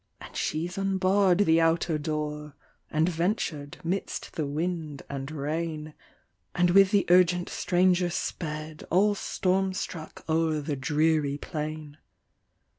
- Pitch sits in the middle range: Yes, medium, 165 Hz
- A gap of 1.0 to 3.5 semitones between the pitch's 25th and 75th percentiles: Yes, average, 3.0 semitones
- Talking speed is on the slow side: Yes, slow, 120 wpm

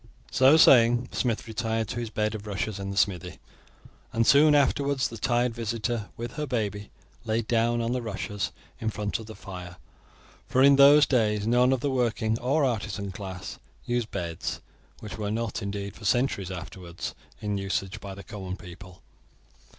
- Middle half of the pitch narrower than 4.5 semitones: Yes, average, 3.3 semitones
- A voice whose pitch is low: Yes, low, 110 Hz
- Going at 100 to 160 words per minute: No, average, 175 wpm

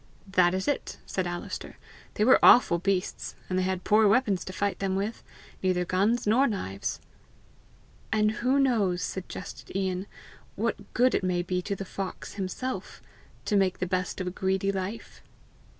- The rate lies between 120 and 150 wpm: No, average, 165 wpm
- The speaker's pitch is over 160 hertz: Yes, high, 190 Hz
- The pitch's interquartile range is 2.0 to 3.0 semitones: Yes, narrow, 2.5 semitones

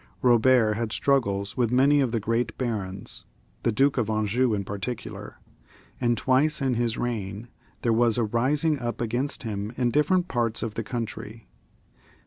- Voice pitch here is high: No, low, 120 Hz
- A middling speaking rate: Yes, average, 160 wpm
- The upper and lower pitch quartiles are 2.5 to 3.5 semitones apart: Yes, average, 3.0 semitones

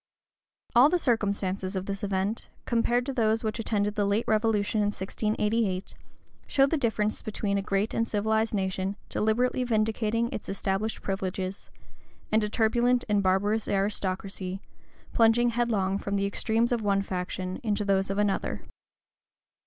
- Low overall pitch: No, high, 210 Hz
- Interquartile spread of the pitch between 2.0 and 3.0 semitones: Yes, narrow, 2.4 semitones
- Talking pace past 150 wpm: No, average, 145 wpm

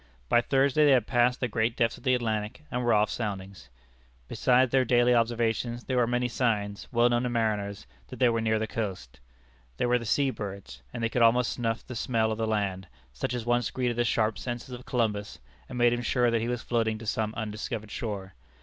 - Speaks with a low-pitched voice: Yes, low, 115 Hz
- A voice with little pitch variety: Yes, narrow, 2.2 semitones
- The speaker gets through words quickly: Yes, fast, 220 wpm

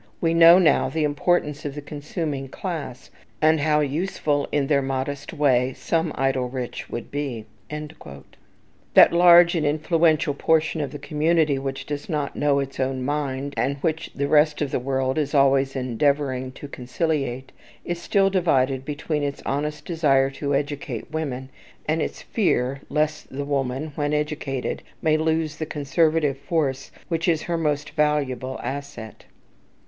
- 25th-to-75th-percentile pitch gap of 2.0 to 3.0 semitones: Yes, average, 2.7 semitones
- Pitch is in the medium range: Yes, medium, 145 Hz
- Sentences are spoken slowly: No, average, 155 wpm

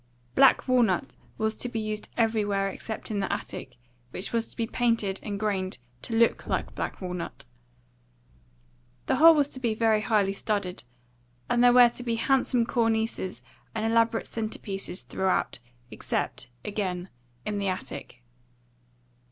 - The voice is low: No, high, 220 Hz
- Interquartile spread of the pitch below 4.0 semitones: Yes, average, 2.9 semitones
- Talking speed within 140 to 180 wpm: Yes, average, 150 wpm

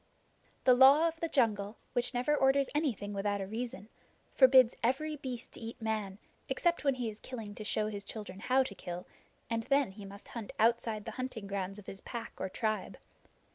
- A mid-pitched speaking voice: No, high, 230 Hz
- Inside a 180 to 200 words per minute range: Yes, average, 195 wpm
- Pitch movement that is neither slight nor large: Yes, average, 4.2 semitones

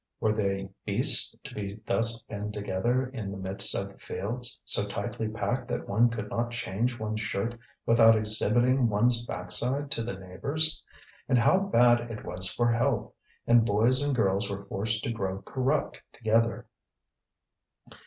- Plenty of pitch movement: No, average, 3.0 semitones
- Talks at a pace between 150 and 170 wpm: Yes, average, 160 wpm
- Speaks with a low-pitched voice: Yes, low, 115 Hz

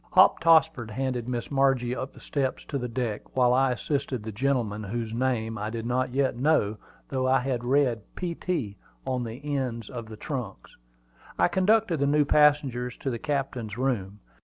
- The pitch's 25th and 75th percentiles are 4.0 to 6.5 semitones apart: No, average, 3.1 semitones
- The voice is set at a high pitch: No, low, 130 Hz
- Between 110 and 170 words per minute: No, average, 185 wpm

